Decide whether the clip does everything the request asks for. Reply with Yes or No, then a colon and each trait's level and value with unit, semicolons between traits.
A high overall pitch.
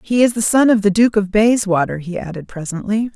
Yes: high, 205 Hz